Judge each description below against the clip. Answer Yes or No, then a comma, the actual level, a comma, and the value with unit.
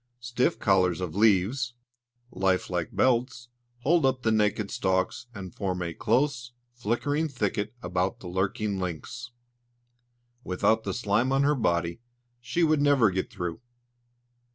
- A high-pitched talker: No, low, 110 Hz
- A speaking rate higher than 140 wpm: No, slow, 135 wpm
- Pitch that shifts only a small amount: No, average, 5.2 semitones